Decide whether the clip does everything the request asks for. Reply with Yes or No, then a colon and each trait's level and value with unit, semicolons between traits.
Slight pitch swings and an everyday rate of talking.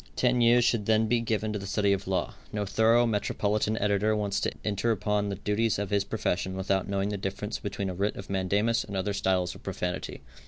No: narrow, 1.9 semitones; fast, 220 wpm